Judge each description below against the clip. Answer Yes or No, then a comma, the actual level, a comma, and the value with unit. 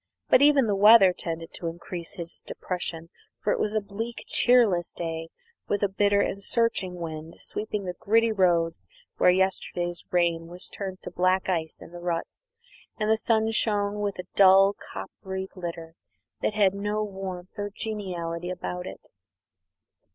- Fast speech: No, average, 160 wpm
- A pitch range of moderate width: Yes, average, 3.2 semitones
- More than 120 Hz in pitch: Yes, high, 190 Hz